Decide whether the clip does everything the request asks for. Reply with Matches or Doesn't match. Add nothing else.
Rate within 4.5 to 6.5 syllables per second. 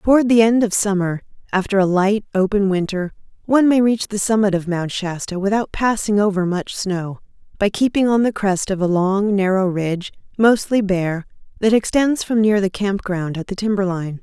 Matches